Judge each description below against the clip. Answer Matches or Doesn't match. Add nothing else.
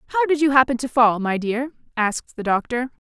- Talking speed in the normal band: Doesn't match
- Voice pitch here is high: Matches